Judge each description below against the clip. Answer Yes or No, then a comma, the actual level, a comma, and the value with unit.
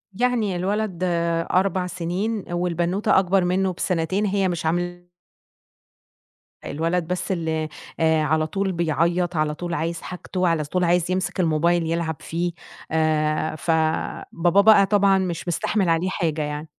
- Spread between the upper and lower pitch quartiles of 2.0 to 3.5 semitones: Yes, narrow, 2.5 semitones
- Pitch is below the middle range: No, medium, 175 Hz